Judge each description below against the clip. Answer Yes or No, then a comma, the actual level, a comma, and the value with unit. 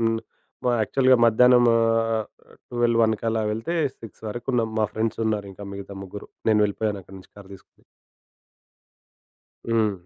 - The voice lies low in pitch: Yes, low, 110 Hz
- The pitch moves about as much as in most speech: No, narrow, 1.9 semitones